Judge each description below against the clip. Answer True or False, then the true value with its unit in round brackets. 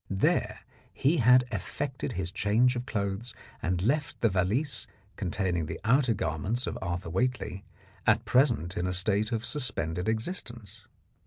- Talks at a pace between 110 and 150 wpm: True (145 wpm)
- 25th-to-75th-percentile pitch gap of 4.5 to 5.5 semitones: True (5.2 semitones)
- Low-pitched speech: True (110 Hz)